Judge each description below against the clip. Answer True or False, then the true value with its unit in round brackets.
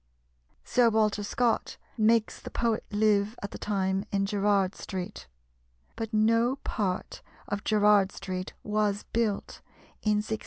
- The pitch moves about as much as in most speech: False (1.7 semitones)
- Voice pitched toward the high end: True (210 Hz)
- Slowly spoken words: True (130 wpm)